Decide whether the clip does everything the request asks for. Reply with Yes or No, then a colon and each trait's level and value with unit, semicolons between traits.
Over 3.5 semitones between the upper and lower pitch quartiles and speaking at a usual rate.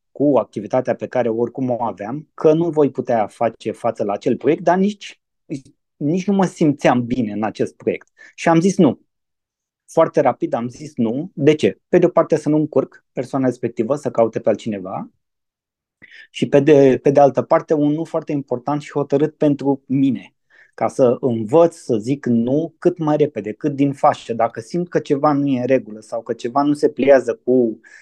No: average, 4.3 semitones; fast, 195 wpm